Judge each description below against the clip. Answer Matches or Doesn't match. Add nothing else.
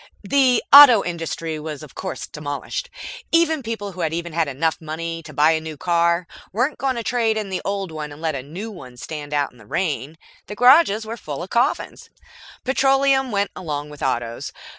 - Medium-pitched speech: Matches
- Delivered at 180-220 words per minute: Matches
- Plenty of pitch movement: Matches